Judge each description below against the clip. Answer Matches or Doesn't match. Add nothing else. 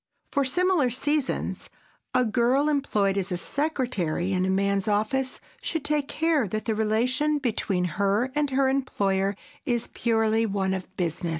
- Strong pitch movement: Matches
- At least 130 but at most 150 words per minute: Matches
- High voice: Matches